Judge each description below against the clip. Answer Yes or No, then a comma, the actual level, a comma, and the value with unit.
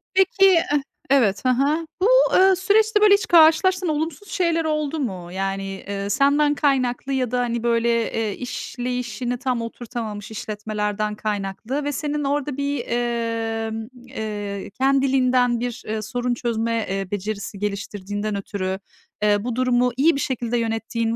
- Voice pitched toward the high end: Yes, high, 240 Hz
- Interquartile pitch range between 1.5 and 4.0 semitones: No, average, 4.8 semitones